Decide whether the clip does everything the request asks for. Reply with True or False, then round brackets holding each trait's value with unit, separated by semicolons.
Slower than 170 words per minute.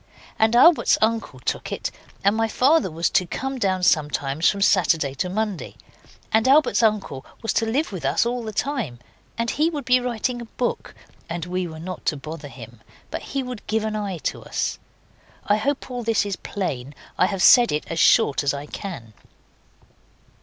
False (190 wpm)